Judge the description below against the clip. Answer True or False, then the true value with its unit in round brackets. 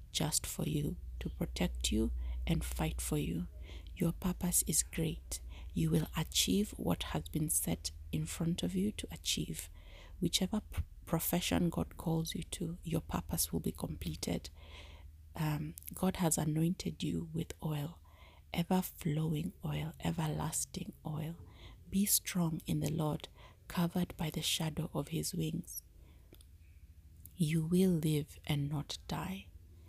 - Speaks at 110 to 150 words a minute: True (140 wpm)